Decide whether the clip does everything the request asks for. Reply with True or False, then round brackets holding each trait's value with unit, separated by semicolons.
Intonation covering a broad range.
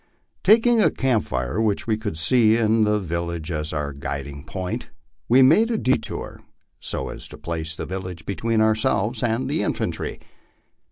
True (6.1 semitones)